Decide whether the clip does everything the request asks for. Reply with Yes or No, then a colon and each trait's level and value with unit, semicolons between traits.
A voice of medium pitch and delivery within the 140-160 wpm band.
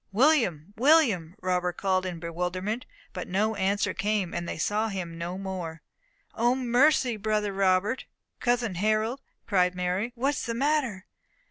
No: high, 200 Hz; average, 145 wpm